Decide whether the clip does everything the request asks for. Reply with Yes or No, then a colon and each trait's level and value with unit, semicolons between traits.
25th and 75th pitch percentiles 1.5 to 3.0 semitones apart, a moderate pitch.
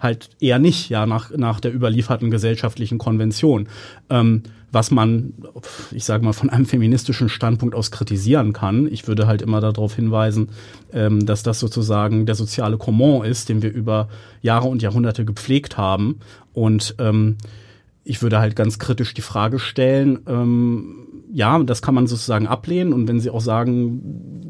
No: narrow, 2.5 semitones; low, 115 Hz